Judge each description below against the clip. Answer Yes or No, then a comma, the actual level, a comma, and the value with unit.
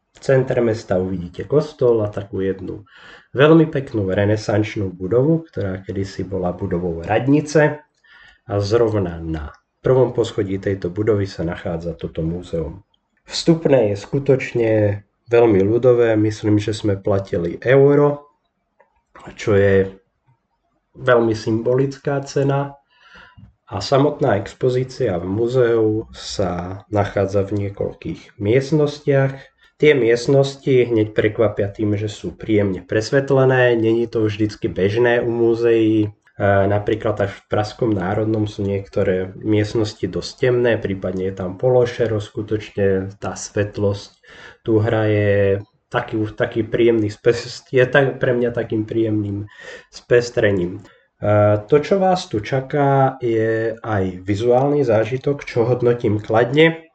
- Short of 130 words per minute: Yes, average, 115 wpm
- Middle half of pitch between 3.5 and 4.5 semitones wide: Yes, average, 4.1 semitones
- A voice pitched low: Yes, low, 110 Hz